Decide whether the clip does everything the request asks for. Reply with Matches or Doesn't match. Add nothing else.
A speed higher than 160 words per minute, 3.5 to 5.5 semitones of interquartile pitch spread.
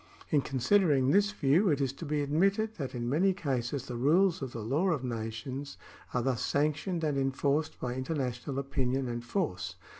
Matches